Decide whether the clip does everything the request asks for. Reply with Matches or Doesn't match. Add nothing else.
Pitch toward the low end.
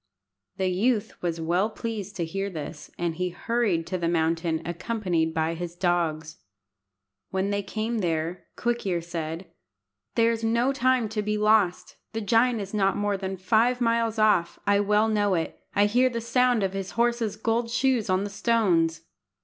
Doesn't match